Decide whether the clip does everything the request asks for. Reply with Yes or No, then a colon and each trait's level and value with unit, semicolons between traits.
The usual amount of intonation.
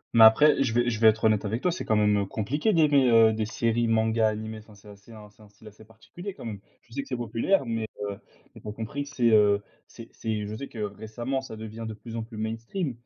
No: narrow, 2.0 semitones